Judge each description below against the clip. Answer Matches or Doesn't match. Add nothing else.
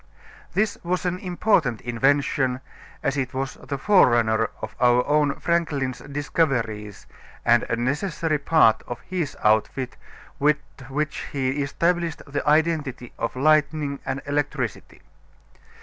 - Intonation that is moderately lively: Matches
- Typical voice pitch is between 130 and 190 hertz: Matches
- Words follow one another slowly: Matches